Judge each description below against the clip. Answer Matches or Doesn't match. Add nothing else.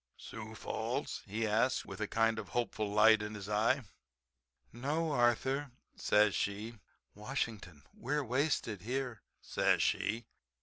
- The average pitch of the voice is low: Matches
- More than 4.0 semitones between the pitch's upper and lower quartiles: Doesn't match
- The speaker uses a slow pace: Matches